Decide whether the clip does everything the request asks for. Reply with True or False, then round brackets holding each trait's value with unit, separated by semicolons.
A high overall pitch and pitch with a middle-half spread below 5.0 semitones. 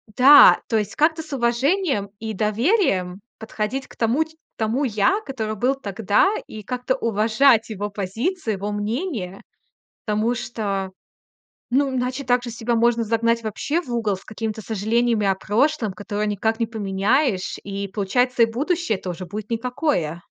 True (225 Hz; 3.7 semitones)